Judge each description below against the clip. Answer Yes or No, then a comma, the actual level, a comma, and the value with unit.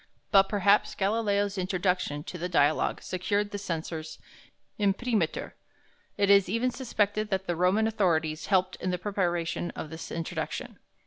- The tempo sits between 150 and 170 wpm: No, average, 140 wpm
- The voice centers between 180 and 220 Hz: Yes, high, 190 Hz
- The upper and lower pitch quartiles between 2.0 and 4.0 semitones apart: Yes, average, 2.9 semitones